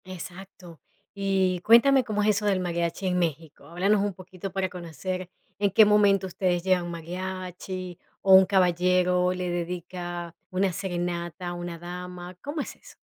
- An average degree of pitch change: No, narrow, 1.7 semitones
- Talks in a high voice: No, medium, 180 Hz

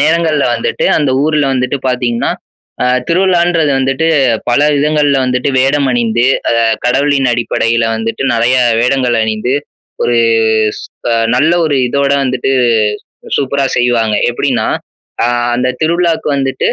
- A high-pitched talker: No, low, 135 Hz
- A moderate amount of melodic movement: Yes, average, 3.4 semitones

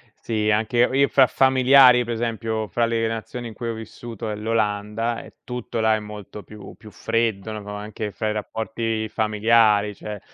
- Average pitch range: No, narrow, 1.7 semitones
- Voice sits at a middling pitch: No, low, 110 Hz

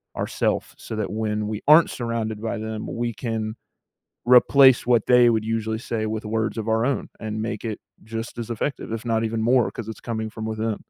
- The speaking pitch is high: No, low, 110 Hz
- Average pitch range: No, narrow, 1.3 semitones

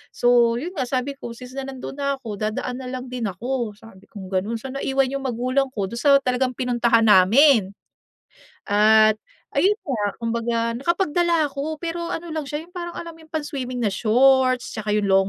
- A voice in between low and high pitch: No, very high, 255 Hz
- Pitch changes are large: No, average, 4.0 semitones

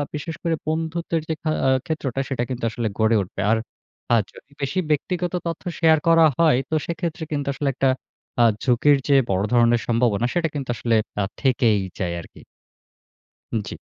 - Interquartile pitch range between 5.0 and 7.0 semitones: Yes, wide, 5.5 semitones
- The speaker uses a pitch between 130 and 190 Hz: Yes, medium, 140 Hz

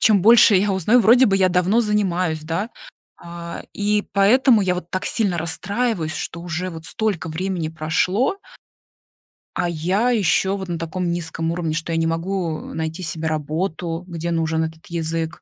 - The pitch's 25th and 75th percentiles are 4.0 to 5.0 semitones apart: No, average, 3.4 semitones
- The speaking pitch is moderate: Yes, medium, 175 Hz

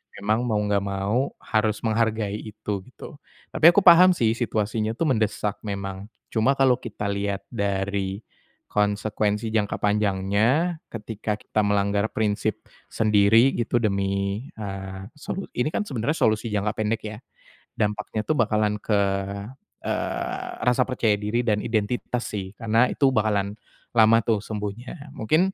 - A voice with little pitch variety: Yes, narrow, 2.3 semitones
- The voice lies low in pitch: Yes, low, 110 Hz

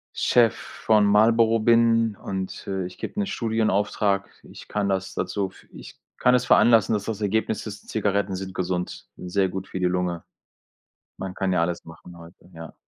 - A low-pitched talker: Yes, low, 100 Hz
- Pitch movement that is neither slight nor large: Yes, average, 3.1 semitones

